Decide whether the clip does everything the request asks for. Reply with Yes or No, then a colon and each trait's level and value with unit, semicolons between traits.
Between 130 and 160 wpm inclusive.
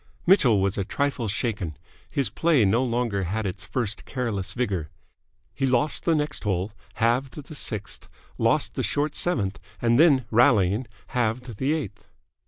Yes: average, 155 wpm